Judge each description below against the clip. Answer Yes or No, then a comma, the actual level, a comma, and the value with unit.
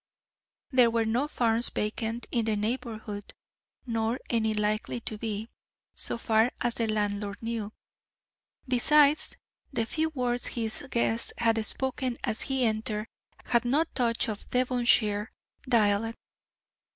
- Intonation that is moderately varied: No, narrow, 2.2 semitones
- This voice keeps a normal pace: No, slow, 130 wpm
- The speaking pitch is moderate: No, high, 230 Hz